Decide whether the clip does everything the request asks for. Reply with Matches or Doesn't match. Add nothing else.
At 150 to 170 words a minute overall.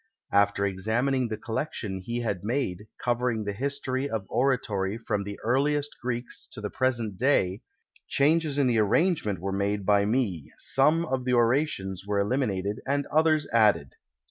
Matches